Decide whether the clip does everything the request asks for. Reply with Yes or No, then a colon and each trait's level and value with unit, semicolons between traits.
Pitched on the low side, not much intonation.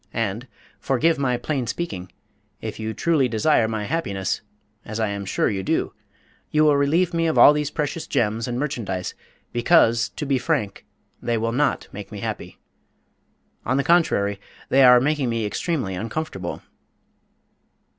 No: low, 125 Hz; wide, 5.6 semitones